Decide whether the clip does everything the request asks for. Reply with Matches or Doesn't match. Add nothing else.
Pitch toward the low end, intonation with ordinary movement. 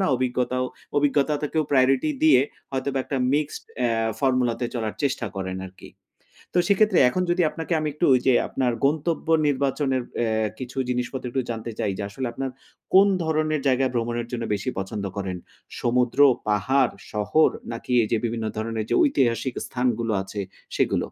Matches